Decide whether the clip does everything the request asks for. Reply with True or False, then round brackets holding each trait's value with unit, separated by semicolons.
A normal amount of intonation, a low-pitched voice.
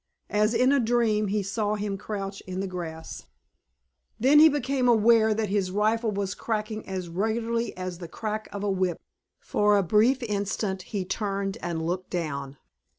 False (3.0 semitones; 210 Hz)